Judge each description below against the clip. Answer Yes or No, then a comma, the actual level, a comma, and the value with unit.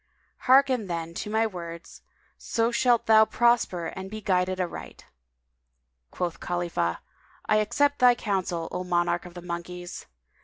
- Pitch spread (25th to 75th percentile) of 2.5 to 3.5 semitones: No, average, 4.3 semitones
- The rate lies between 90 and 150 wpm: Yes, average, 145 wpm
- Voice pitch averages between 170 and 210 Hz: Yes, medium, 185 Hz